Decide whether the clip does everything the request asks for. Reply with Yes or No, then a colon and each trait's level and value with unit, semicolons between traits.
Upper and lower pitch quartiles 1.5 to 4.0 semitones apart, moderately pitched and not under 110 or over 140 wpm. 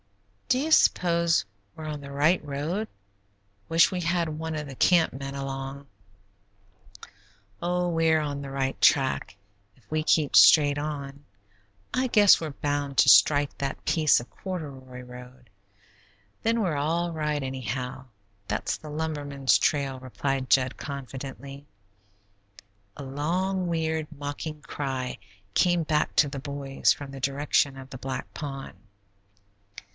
Yes: average, 2.9 semitones; medium, 145 Hz; slow, 135 wpm